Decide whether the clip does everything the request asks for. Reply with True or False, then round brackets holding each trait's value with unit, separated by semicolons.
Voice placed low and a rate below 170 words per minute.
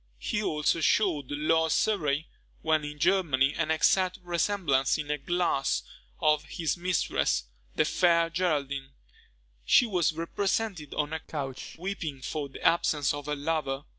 False (155 Hz; 140 wpm)